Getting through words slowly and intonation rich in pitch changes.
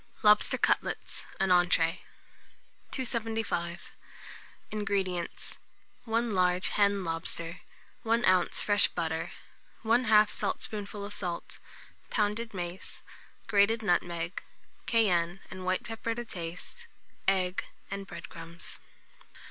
No: slow, 100 wpm; average, 3.8 semitones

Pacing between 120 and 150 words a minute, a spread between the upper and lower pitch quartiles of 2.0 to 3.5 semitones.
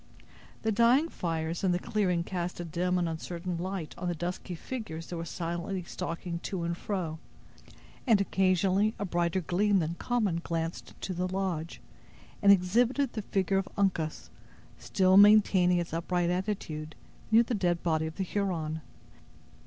No: average, 160 wpm; average, 2.8 semitones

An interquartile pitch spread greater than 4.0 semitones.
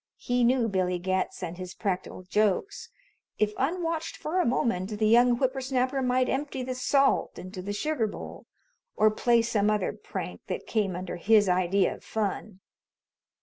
Yes: average, 5.2 semitones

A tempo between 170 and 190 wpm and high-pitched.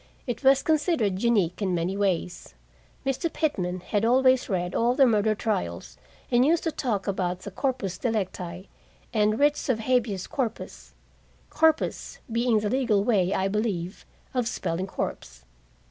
No: average, 145 wpm; high, 215 Hz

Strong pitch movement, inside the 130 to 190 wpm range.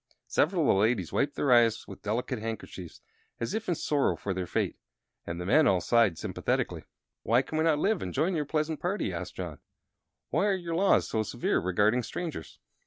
No: wide, 7.5 semitones; average, 200 wpm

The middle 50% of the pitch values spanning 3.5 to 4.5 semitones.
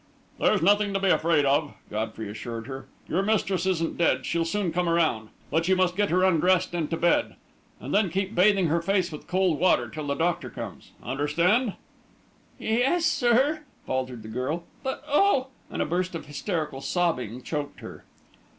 No: average, 4.9 semitones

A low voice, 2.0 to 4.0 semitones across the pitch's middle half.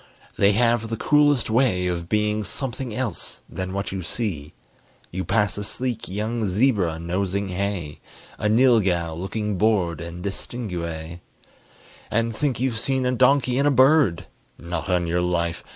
No: low, 105 Hz; average, 5.2 semitones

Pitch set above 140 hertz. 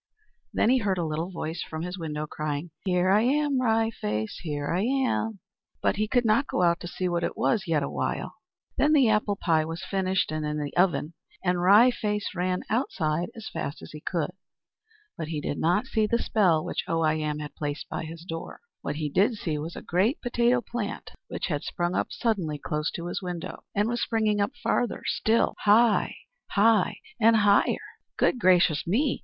Yes: medium, 185 Hz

